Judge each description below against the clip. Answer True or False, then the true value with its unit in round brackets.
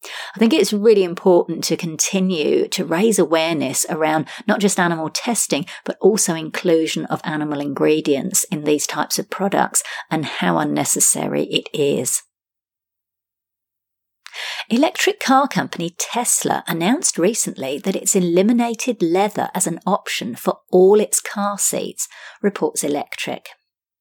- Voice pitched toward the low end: False (175 Hz)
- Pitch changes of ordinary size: False (5.8 semitones)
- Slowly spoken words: True (125 wpm)